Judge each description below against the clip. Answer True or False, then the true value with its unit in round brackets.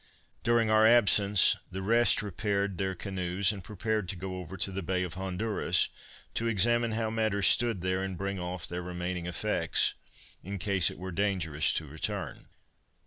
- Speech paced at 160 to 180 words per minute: True (170 wpm)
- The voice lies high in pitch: False (95 Hz)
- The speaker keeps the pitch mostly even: False (3.1 semitones)